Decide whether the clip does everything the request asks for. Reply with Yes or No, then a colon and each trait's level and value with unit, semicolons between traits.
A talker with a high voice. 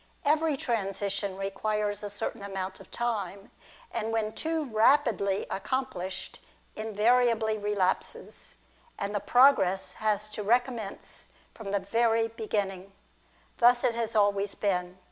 Yes: high, 215 Hz